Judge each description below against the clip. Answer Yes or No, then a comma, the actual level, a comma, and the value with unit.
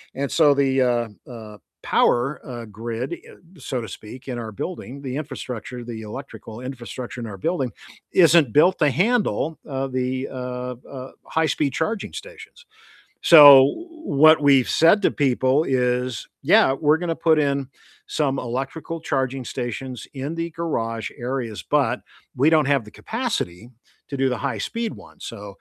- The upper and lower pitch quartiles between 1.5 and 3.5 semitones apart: No, average, 4.0 semitones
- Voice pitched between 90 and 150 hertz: Yes, low, 135 Hz